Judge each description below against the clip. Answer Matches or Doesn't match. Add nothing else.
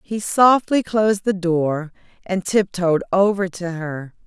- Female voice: Matches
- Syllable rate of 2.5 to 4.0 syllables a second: Matches